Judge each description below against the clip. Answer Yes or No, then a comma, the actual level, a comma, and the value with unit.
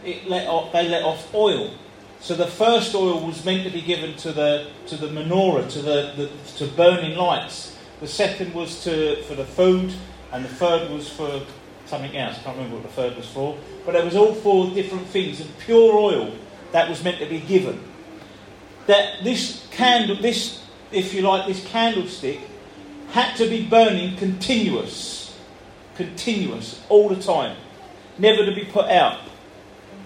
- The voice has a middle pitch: Yes, medium, 180 Hz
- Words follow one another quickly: No, average, 175 wpm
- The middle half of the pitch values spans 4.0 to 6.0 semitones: Yes, average, 4.8 semitones